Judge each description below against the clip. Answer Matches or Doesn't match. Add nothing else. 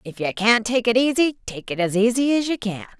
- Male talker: Doesn't match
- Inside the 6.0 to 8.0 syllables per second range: Doesn't match